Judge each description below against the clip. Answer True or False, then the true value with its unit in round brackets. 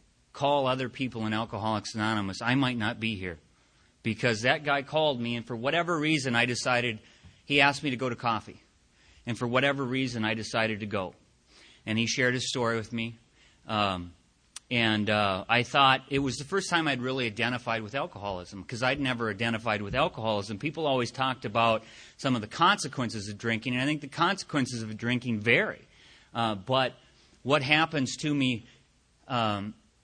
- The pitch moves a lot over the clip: False (3.3 semitones)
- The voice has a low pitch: True (120 Hz)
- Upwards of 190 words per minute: False (180 wpm)